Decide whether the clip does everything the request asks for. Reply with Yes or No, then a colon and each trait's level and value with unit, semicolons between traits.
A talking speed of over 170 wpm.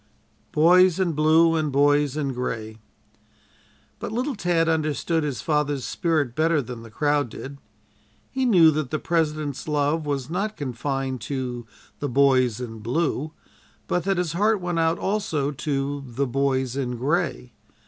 No: average, 150 wpm